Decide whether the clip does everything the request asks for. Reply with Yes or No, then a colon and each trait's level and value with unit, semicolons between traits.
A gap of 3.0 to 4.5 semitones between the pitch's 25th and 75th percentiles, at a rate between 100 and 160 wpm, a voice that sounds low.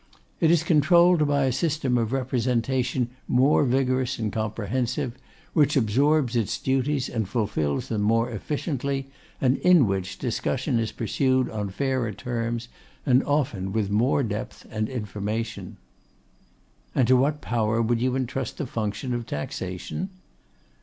Yes: average, 3.5 semitones; average, 140 wpm; low, 125 Hz